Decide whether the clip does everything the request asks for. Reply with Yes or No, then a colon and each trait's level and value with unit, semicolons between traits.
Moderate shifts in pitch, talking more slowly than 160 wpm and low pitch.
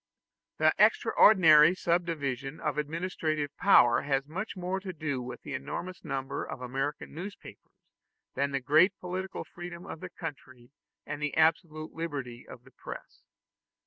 No: average, 4.2 semitones; average, 145 wpm; medium, 155 Hz